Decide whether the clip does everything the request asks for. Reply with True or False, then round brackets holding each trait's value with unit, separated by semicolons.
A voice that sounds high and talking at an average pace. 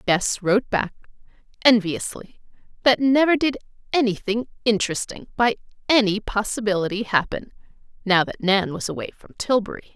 False (215 Hz; 120 wpm)